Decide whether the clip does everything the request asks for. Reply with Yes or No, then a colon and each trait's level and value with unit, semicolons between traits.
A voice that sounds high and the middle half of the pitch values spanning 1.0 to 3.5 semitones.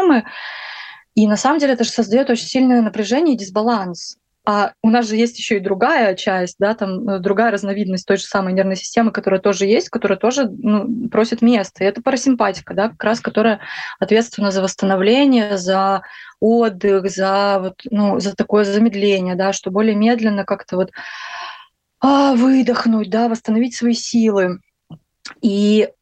Yes: high, 215 Hz; average, 3.1 semitones